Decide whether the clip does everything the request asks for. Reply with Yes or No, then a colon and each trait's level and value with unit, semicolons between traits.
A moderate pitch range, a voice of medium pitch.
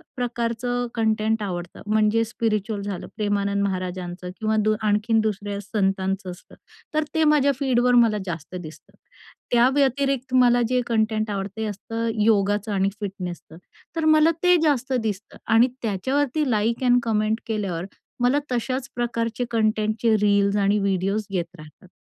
No: average, 3.4 semitones; high, 215 Hz